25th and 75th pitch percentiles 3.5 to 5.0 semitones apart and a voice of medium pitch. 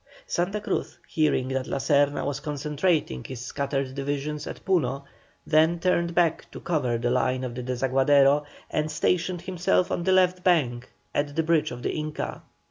Yes: average, 4.2 semitones; medium, 150 Hz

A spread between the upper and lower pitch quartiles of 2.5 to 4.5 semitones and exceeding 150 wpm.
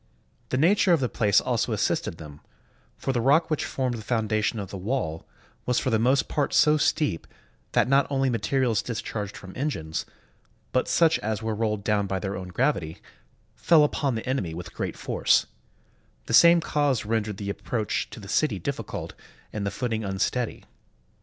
No: average, 5.1 semitones; average, 180 wpm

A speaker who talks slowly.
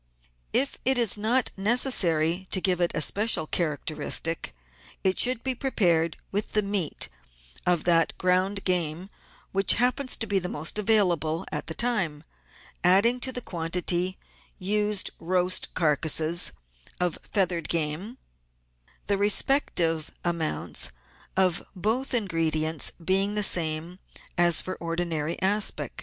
Yes: slow, 125 wpm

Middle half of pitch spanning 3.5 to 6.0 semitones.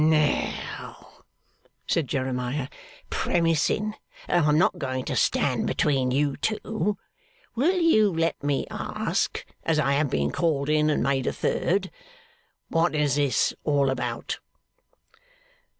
Yes: average, 3.9 semitones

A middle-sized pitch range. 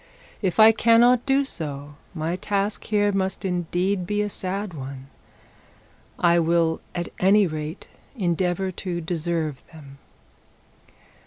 Yes: average, 3.9 semitones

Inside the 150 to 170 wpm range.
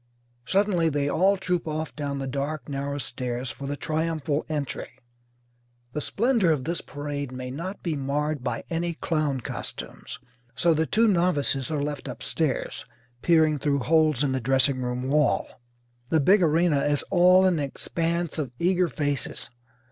Yes: average, 155 wpm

